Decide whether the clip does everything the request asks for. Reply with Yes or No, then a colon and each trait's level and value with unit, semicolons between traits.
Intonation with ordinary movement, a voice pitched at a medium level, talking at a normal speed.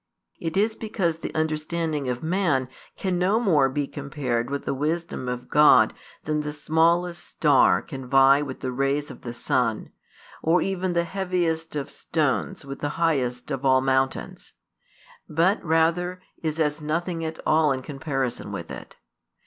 Yes: average, 3.8 semitones; medium, 155 Hz; average, 160 wpm